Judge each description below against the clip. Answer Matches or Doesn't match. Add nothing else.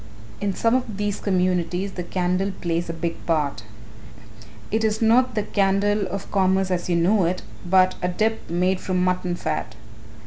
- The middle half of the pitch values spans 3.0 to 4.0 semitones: Doesn't match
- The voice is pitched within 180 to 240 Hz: Matches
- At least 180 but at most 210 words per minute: Doesn't match